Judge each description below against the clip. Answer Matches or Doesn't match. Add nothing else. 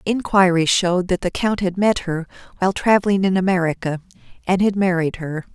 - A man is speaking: Doesn't match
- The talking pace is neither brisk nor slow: Matches